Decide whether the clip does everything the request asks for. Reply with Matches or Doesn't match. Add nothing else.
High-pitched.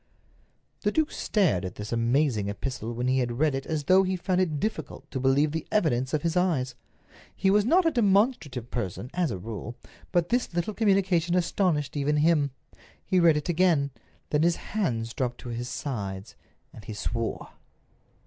Doesn't match